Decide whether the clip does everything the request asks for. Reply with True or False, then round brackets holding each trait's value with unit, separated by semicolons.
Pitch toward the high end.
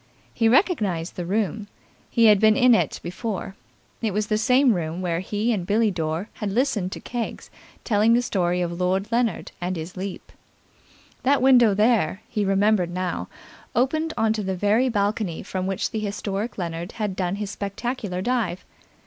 True (205 Hz)